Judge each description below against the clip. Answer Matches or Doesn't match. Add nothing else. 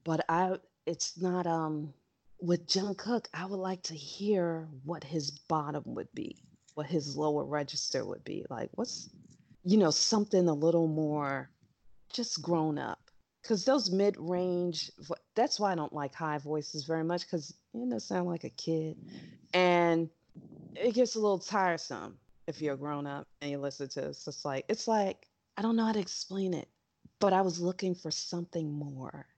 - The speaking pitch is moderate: Matches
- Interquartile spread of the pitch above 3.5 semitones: Matches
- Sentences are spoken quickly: Doesn't match